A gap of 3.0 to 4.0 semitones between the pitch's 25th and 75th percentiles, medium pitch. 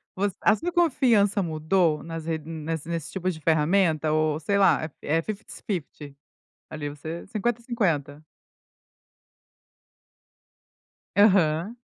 No: average, 4.5 semitones; medium, 165 Hz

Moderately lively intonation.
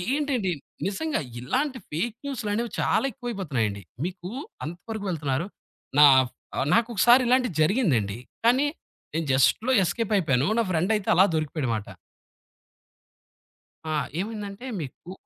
No: wide, 7.9 semitones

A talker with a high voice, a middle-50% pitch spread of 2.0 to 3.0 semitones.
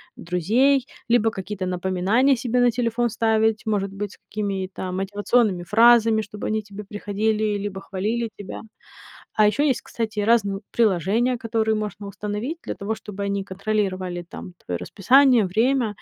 Yes: high, 210 Hz; average, 2.7 semitones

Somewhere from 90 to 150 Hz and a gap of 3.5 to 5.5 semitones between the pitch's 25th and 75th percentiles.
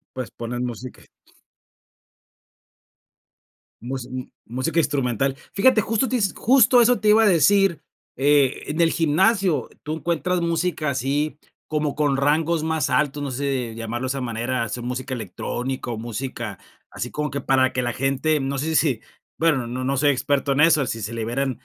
Yes: medium, 140 Hz; average, 4.2 semitones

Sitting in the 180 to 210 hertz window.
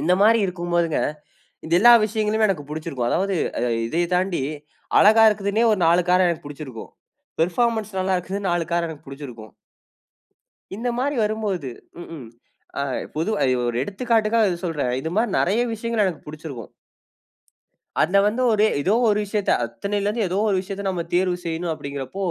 Yes: medium, 185 Hz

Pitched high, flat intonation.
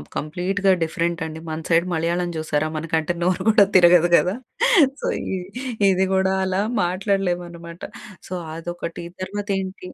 No: medium, 175 Hz; narrow, 2.3 semitones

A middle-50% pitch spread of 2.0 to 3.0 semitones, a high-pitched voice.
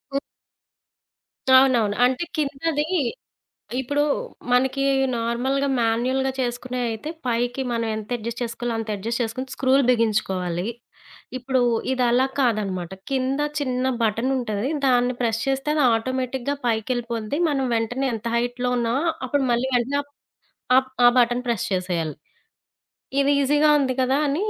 Yes: narrow, 2.6 semitones; high, 245 Hz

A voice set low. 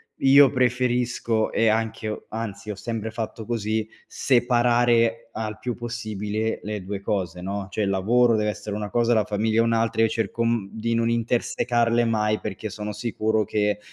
Yes: low, 110 Hz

